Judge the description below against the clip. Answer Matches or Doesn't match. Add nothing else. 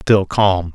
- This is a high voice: Doesn't match